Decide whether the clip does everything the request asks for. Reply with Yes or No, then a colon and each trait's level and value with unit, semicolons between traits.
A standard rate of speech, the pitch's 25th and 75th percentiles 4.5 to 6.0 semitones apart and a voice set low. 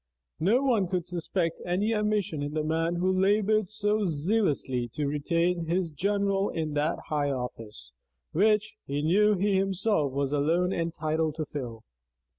No: average, 150 wpm; average, 5.0 semitones; medium, 170 Hz